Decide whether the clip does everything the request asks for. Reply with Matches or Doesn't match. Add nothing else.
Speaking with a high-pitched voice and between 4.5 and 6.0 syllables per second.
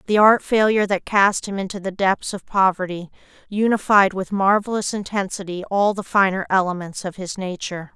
Matches